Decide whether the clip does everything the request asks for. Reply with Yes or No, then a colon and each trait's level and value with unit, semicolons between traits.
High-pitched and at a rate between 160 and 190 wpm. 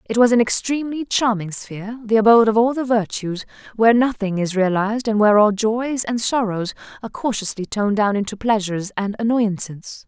Yes: high, 215 Hz; average, 180 wpm